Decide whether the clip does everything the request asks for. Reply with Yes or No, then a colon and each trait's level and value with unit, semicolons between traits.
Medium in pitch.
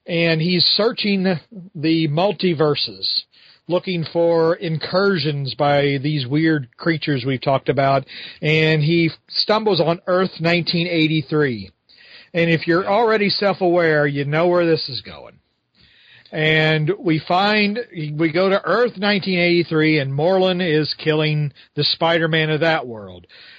Yes: medium, 165 Hz